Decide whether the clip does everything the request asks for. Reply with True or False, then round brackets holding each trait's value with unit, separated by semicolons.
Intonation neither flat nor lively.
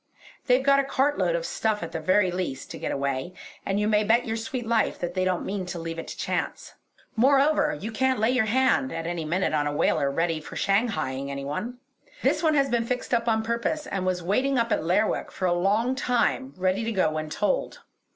False (6.2 semitones)